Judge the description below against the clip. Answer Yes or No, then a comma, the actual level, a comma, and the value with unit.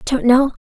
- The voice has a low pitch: No, very high, 260 Hz